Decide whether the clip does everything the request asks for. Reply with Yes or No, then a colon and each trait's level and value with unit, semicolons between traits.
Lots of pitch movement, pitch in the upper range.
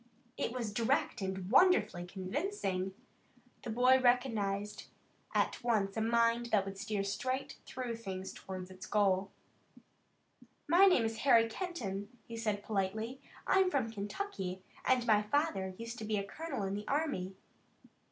No: average, 4.4 semitones; high, 220 Hz